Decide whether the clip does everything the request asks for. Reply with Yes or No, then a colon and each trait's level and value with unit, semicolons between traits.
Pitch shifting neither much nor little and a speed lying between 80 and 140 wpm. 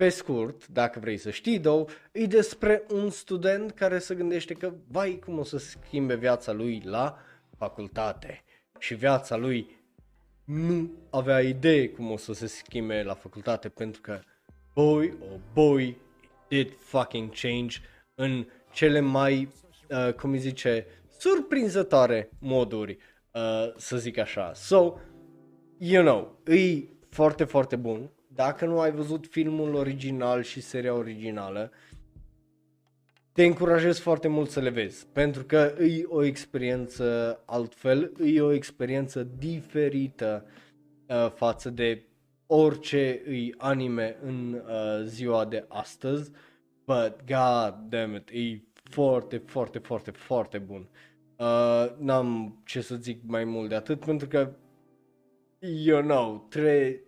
Yes: average, 5.0 semitones; average, 135 wpm